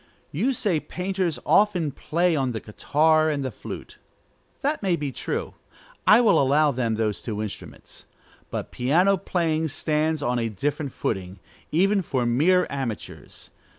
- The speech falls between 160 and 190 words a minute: No, average, 150 wpm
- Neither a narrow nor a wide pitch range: No, wide, 6.2 semitones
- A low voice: No, medium, 150 Hz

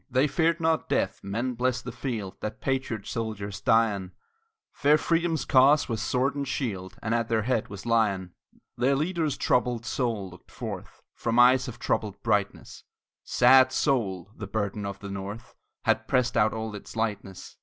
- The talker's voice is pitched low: Yes, low, 115 Hz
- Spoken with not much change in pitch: No, average, 4.2 semitones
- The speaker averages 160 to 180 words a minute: Yes, average, 170 wpm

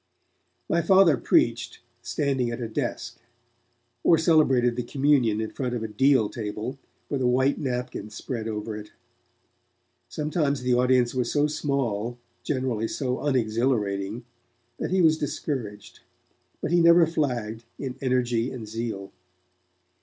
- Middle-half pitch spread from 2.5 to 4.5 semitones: Yes, average, 4.0 semitones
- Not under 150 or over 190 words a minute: No, slow, 135 wpm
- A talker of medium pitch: No, low, 125 Hz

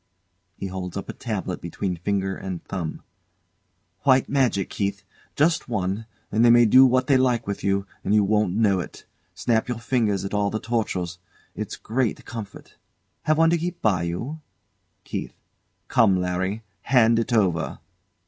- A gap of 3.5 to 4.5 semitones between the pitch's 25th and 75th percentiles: Yes, average, 4.2 semitones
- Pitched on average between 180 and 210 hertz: No, low, 110 Hz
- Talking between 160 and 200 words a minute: Yes, average, 165 wpm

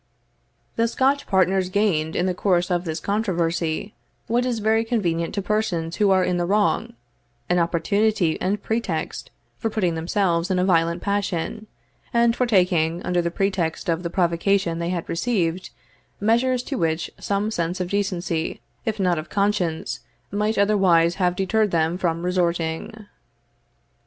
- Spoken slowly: No, average, 155 wpm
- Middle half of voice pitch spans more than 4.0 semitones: No, average, 3.7 semitones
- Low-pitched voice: No, medium, 185 Hz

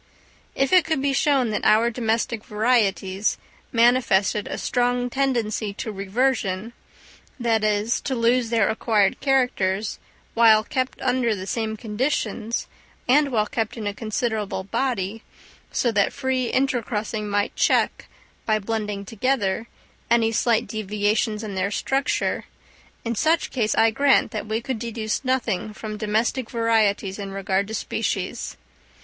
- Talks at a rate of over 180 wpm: No, slow, 135 wpm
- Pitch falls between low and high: No, high, 225 Hz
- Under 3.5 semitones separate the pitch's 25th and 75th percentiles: Yes, average, 2.9 semitones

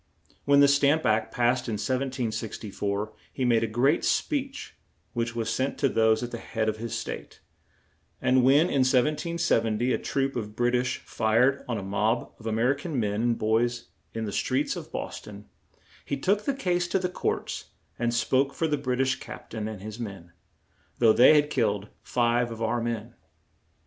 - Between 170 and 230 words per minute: Yes, average, 190 wpm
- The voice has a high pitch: No, low, 120 Hz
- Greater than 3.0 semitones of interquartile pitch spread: Yes, average, 3.7 semitones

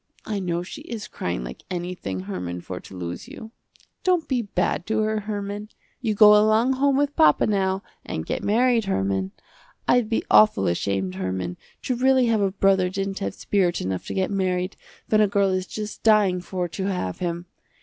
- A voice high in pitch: Yes, high, 195 Hz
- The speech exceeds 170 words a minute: Yes, average, 190 wpm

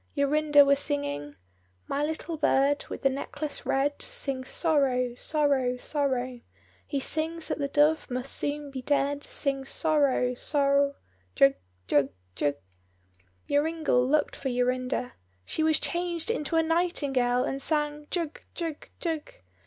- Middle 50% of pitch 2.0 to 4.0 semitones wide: Yes, average, 3.3 semitones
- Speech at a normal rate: No, slow, 130 wpm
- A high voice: Yes, very high, 285 Hz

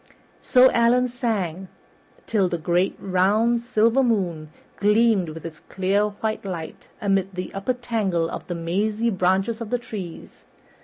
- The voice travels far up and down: No, average, 4.2 semitones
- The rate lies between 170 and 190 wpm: No, average, 145 wpm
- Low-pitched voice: No, high, 200 Hz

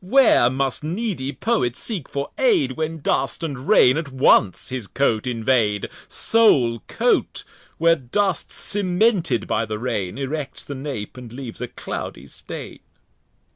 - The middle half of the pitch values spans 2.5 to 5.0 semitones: No, wide, 5.6 semitones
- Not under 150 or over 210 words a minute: No, average, 140 wpm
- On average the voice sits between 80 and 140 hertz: Yes, low, 135 Hz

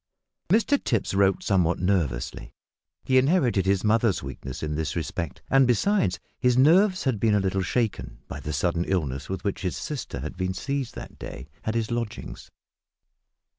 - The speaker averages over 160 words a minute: Yes, average, 170 wpm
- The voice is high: No, low, 100 Hz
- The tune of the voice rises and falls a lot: Yes, wide, 6.6 semitones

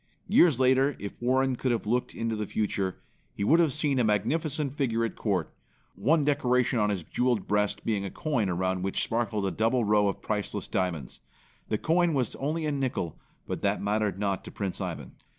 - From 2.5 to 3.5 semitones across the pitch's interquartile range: No, average, 4.8 semitones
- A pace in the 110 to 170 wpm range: No, average, 195 wpm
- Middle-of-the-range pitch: No, low, 115 Hz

